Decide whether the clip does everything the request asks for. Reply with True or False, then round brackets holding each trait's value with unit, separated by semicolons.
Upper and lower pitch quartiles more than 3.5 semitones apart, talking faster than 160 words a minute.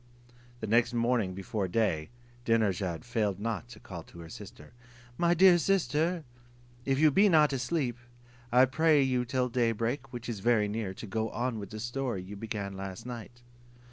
True (4.1 semitones; 175 wpm)